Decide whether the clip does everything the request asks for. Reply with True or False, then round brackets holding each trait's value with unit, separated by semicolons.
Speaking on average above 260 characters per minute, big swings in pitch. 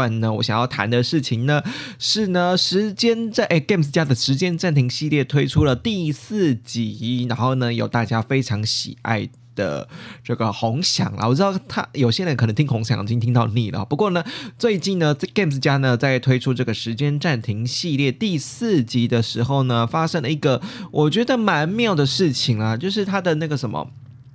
True (300 characters per minute; 6.2 semitones)